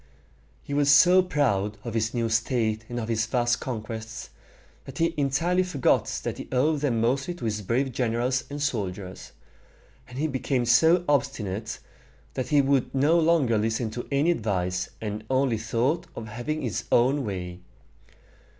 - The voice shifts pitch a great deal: No, average, 4.4 semitones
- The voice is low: Yes, low, 125 Hz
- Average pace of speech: Yes, average, 160 wpm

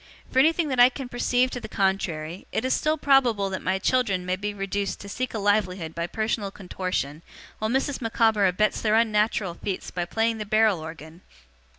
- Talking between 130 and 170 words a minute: No, average, 195 wpm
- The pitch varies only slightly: No, average, 4.1 semitones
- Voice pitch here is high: Yes, high, 210 Hz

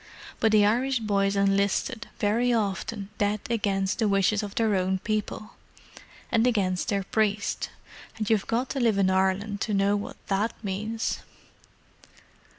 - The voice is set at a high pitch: Yes, high, 205 Hz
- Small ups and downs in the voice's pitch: Yes, narrow, 2.0 semitones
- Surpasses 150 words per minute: No, average, 145 wpm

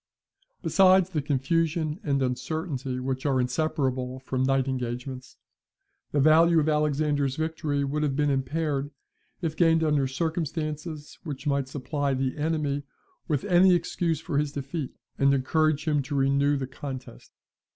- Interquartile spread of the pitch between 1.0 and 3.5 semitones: Yes, average, 2.9 semitones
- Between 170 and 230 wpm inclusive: No, average, 140 wpm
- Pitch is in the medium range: Yes, medium, 145 Hz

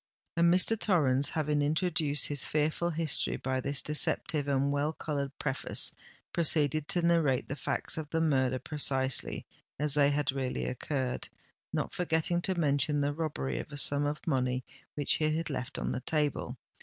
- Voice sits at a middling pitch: Yes, medium, 145 Hz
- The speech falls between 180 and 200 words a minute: No, average, 165 wpm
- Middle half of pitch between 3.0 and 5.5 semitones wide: No, narrow, 2.5 semitones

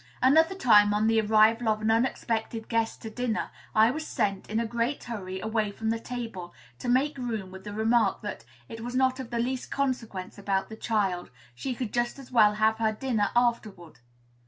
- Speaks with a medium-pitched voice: No, high, 225 Hz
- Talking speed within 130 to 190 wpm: No, average, 200 wpm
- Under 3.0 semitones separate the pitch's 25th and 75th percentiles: Yes, narrow, 2.6 semitones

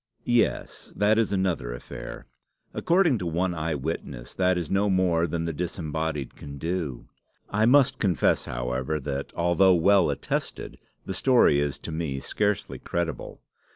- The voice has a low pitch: Yes, very low, 85 Hz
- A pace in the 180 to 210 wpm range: No, average, 145 wpm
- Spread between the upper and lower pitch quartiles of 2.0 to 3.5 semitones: No, average, 4.8 semitones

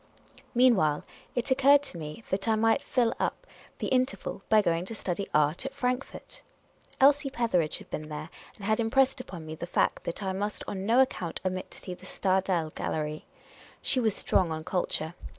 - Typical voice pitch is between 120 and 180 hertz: No, high, 200 Hz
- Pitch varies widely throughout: Yes, wide, 6.8 semitones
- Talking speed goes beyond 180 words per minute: Yes, average, 190 wpm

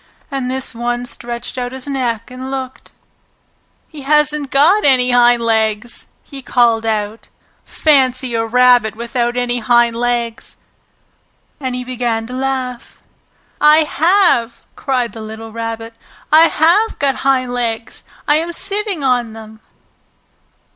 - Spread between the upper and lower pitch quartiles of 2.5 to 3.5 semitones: Yes, average, 2.8 semitones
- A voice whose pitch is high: Yes, very high, 250 Hz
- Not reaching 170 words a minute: Yes, slow, 135 wpm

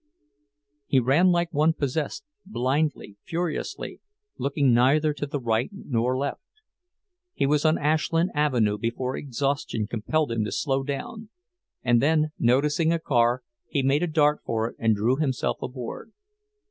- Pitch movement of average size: Yes, average, 4.2 semitones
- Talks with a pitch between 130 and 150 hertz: Yes, medium, 140 Hz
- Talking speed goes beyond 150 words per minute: No, average, 145 wpm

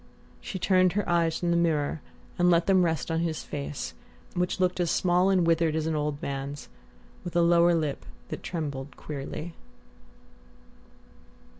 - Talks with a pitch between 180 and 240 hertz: No, medium, 170 Hz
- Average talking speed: Yes, average, 160 wpm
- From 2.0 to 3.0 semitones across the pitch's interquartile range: Yes, narrow, 2.6 semitones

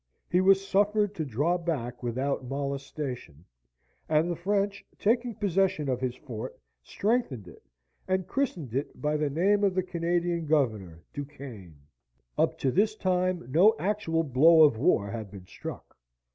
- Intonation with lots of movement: Yes, wide, 6.7 semitones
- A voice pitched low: No, medium, 160 Hz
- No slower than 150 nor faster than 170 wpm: Yes, average, 155 wpm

